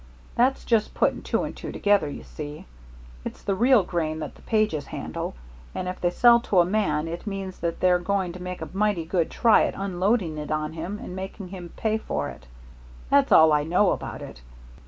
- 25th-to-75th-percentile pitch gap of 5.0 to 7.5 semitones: No, average, 4.2 semitones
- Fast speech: Yes, fast, 210 wpm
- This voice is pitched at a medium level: Yes, medium, 180 Hz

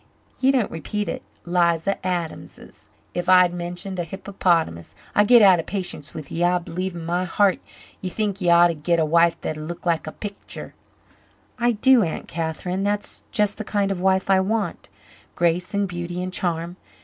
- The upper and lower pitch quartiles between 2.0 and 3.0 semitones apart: Yes, average, 2.7 semitones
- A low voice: No, medium, 180 Hz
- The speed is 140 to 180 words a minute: No, average, 190 wpm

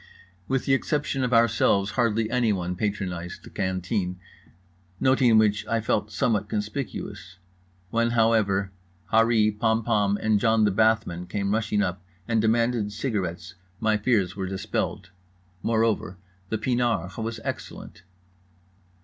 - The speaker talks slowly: Yes, slow, 125 wpm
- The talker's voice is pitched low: Yes, low, 110 Hz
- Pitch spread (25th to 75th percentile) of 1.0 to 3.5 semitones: Yes, average, 2.8 semitones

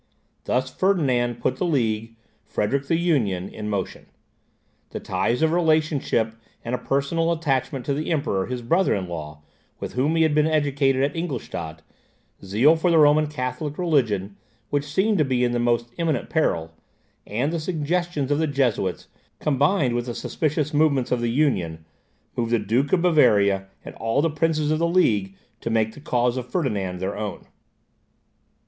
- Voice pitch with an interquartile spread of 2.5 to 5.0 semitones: No, wide, 5.5 semitones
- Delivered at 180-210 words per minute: No, average, 170 wpm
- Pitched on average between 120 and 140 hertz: Yes, low, 135 Hz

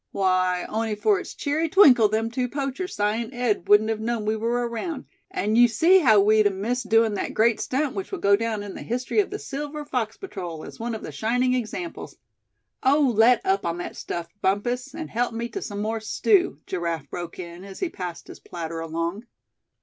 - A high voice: Yes, high, 225 Hz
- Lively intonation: No, average, 4.0 semitones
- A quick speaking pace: Yes, fast, 215 wpm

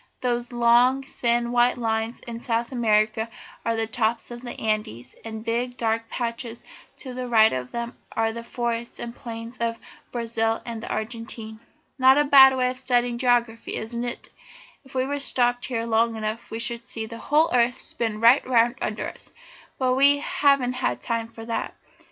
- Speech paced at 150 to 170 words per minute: No, average, 180 wpm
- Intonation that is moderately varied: No, narrow, 1.5 semitones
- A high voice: Yes, high, 235 Hz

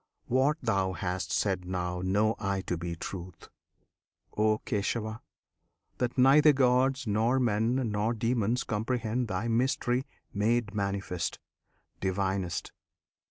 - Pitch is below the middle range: Yes, low, 110 Hz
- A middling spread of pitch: Yes, average, 4.4 semitones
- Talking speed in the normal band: No, slow, 115 wpm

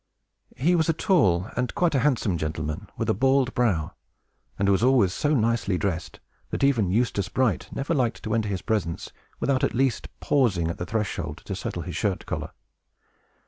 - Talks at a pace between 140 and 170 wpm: No, average, 185 wpm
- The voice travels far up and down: Yes, wide, 6.1 semitones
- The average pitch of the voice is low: Yes, low, 115 Hz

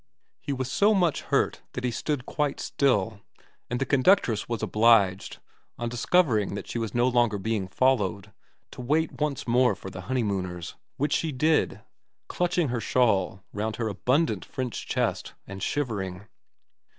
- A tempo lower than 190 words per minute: Yes, average, 155 wpm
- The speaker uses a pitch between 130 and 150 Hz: No, low, 120 Hz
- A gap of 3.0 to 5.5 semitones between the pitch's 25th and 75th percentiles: Yes, average, 5.2 semitones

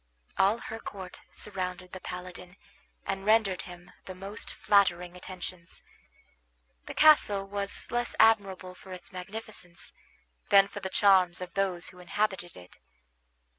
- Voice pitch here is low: No, high, 190 Hz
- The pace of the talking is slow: Yes, slow, 130 wpm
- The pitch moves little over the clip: Yes, narrow, 1.9 semitones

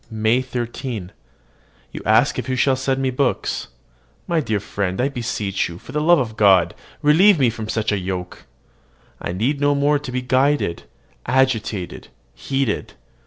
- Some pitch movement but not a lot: Yes, average, 4.6 semitones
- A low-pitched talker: Yes, low, 125 Hz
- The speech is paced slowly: No, average, 165 wpm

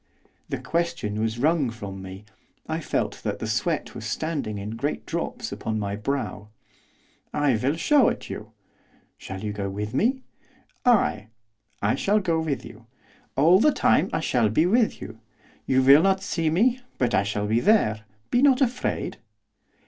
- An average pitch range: No, wide, 8.6 semitones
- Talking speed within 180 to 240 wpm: No, average, 170 wpm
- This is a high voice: No, low, 135 Hz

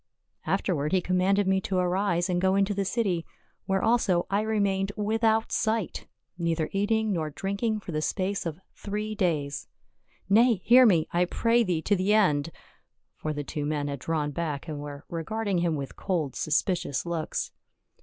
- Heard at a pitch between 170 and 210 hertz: Yes, medium, 185 Hz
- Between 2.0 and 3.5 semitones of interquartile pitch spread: No, average, 4.5 semitones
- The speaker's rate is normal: Yes, average, 180 wpm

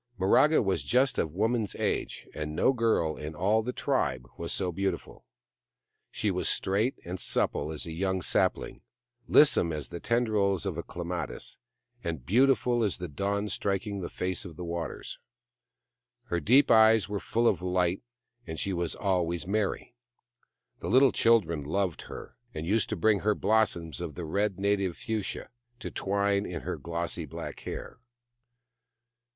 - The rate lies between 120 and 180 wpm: Yes, average, 160 wpm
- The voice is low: Yes, very low, 95 Hz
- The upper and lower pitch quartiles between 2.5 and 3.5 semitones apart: No, average, 4.3 semitones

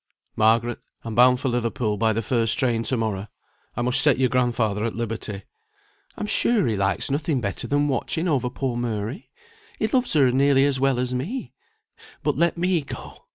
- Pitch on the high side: No, low, 125 Hz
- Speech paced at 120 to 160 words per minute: No, average, 185 wpm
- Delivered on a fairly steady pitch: No, average, 3.7 semitones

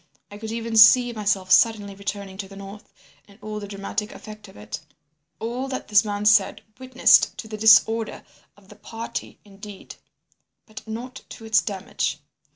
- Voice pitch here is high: Yes, high, 210 Hz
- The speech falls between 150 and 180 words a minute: Yes, average, 165 wpm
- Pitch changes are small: Yes, narrow, 1.9 semitones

